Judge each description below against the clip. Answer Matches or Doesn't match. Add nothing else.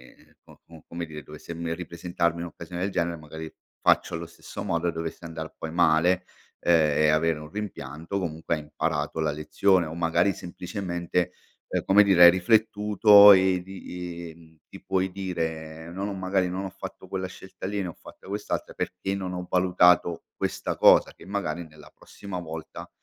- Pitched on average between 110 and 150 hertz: Doesn't match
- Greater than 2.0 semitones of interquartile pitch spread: Matches